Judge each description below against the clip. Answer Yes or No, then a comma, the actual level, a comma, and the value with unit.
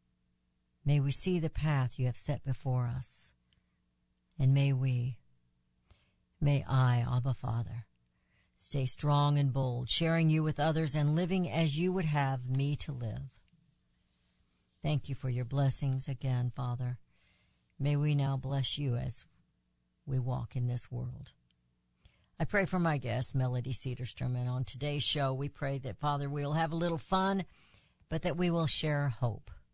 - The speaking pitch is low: Yes, low, 130 Hz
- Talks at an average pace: Yes, average, 160 wpm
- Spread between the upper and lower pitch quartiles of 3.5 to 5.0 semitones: No, average, 3.1 semitones